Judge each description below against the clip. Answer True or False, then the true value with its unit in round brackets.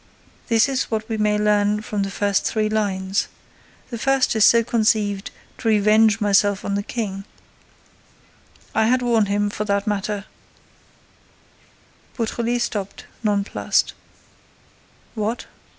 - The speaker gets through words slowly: True (125 wpm)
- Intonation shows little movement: True (1.8 semitones)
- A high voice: True (210 Hz)